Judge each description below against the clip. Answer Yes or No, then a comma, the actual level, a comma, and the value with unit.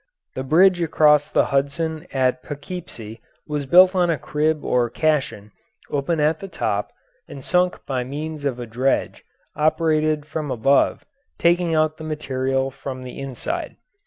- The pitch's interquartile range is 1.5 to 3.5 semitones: Yes, average, 3.1 semitones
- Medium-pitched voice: Yes, medium, 150 Hz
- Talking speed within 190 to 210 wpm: No, average, 150 wpm